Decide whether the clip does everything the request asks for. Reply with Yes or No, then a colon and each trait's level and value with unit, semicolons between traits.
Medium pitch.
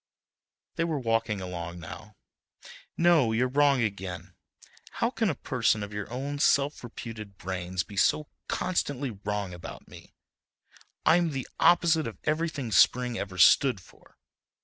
No: low, 115 Hz